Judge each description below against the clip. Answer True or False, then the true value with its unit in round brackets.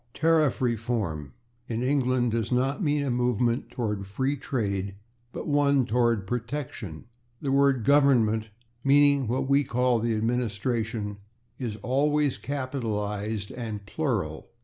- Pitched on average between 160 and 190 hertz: False (125 Hz)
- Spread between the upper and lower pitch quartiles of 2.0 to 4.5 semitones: True (4.1 semitones)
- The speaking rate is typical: False (125 wpm)